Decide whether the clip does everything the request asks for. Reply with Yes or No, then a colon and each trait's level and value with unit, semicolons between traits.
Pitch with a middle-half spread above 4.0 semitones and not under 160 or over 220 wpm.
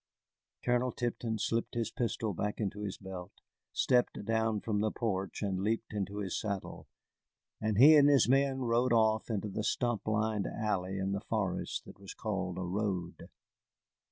No: average, 3.0 semitones; average, 165 wpm